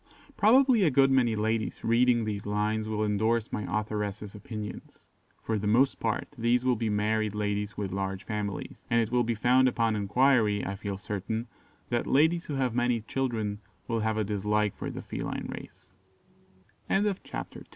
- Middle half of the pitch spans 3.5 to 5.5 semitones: No, average, 2.7 semitones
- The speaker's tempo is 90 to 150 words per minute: Yes, average, 145 wpm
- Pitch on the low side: Yes, low, 110 Hz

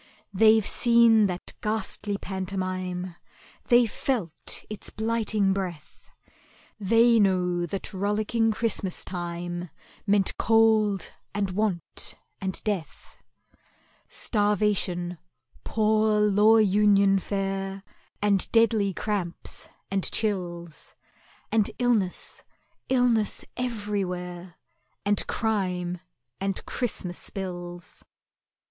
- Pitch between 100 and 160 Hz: No, high, 200 Hz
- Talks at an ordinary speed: No, slow, 80 wpm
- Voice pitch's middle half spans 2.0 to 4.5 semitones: Yes, average, 3.0 semitones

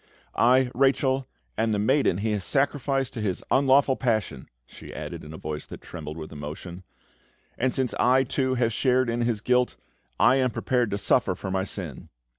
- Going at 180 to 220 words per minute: Yes, average, 185 wpm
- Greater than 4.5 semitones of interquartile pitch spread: Yes, wide, 5.5 semitones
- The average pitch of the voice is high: No, low, 120 Hz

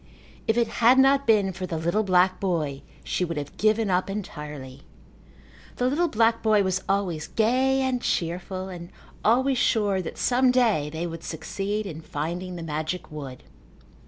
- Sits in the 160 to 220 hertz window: Yes, high, 190 Hz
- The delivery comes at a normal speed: Yes, average, 165 wpm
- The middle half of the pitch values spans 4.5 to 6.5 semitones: Yes, wide, 5.4 semitones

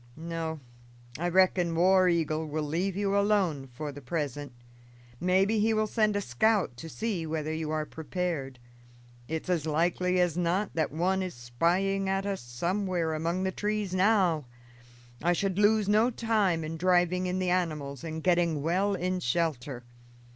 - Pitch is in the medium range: Yes, medium, 175 Hz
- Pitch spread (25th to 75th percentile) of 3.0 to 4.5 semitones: Yes, average, 3.4 semitones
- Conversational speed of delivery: Yes, average, 160 wpm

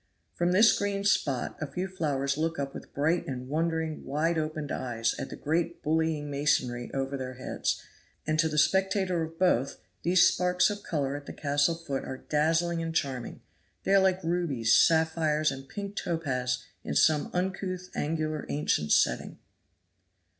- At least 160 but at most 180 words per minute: Yes, average, 165 wpm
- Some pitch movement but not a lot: Yes, average, 3.8 semitones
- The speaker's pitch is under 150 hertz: No, medium, 155 Hz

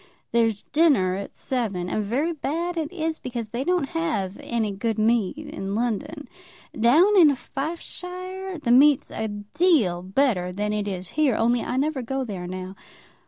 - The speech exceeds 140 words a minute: Yes, average, 165 wpm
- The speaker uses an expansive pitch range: Yes, wide, 7.0 semitones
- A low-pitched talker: No, high, 240 Hz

